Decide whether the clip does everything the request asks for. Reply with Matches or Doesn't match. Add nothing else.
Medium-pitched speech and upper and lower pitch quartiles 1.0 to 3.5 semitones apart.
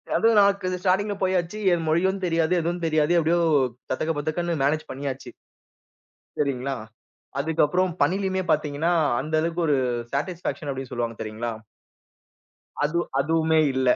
Doesn't match